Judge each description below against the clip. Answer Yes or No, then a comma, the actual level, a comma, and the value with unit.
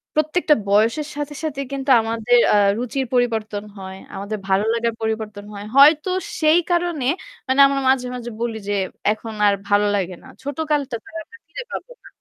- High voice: Yes, high, 245 Hz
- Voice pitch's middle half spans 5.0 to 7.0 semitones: Yes, average, 5.3 semitones